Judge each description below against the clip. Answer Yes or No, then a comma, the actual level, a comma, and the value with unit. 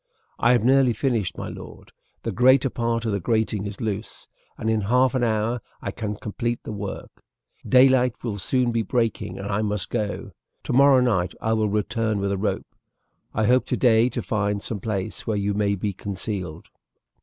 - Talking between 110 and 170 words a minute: No, average, 185 wpm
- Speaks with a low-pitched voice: Yes, low, 110 Hz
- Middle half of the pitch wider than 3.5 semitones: No, average, 3.0 semitones